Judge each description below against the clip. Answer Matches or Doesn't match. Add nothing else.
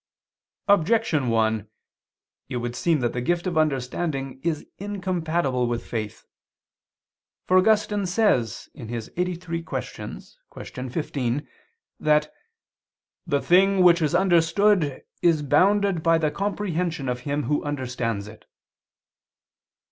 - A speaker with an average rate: Doesn't match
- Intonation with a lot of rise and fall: Matches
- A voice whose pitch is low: Doesn't match